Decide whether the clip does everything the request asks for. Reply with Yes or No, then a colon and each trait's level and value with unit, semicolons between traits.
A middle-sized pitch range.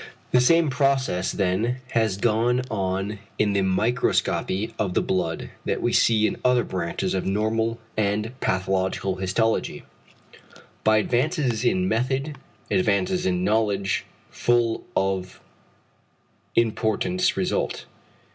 Yes: average, 4.3 semitones